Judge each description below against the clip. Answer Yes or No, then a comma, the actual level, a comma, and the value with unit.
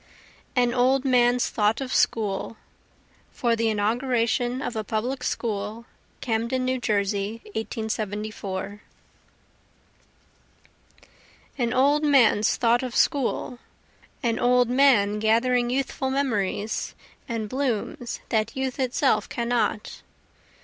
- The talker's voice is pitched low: No, high, 235 Hz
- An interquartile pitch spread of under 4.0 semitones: Yes, average, 2.8 semitones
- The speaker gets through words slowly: Yes, slow, 100 wpm